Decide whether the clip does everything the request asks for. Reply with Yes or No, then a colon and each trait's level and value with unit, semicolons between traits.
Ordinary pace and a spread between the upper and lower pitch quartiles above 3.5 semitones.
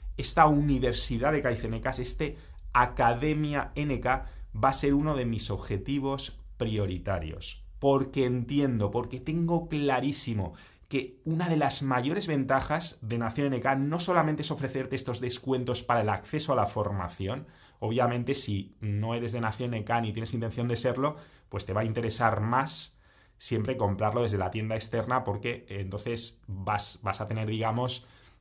Yes: average, 155 wpm; average, 3.9 semitones